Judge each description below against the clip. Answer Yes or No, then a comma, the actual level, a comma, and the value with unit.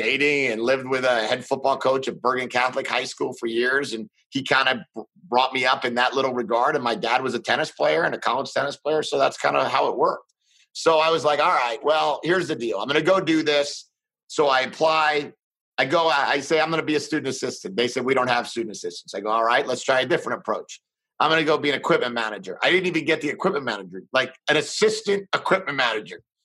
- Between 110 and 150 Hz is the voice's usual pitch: Yes, medium, 140 Hz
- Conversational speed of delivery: No, fast, 250 wpm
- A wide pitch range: No, average, 3.8 semitones